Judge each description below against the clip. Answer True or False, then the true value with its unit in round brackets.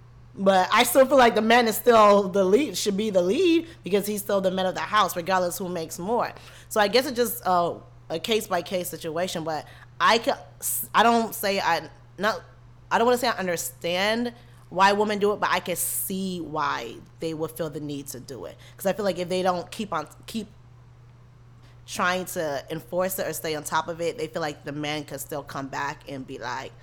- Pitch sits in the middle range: True (175 Hz)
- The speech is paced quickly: True (230 wpm)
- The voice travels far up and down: True (6.0 semitones)